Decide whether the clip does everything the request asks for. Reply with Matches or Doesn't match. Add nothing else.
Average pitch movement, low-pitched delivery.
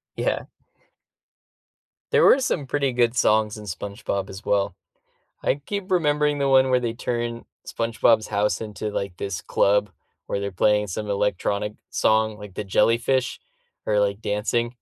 Matches